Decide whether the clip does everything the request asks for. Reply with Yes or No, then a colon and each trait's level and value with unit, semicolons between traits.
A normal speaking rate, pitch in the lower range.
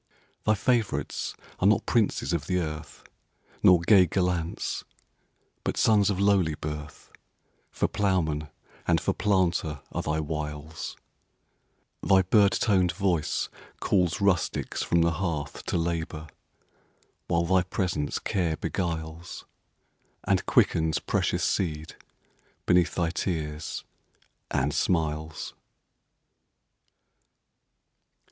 No: slow, 95 wpm; very low, 85 Hz